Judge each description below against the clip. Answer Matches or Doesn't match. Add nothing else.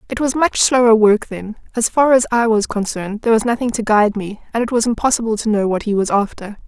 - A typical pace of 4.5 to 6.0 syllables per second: Doesn't match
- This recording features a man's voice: Doesn't match